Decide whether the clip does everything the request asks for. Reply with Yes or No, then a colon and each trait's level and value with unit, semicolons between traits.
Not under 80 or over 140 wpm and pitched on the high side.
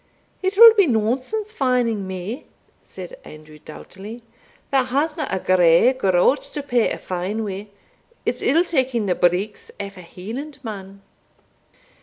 Yes: slow, 135 wpm; high, 225 Hz